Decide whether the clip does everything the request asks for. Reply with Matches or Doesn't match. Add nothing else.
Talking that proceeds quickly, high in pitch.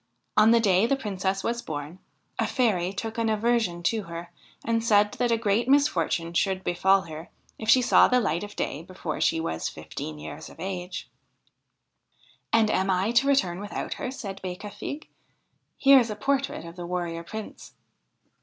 Doesn't match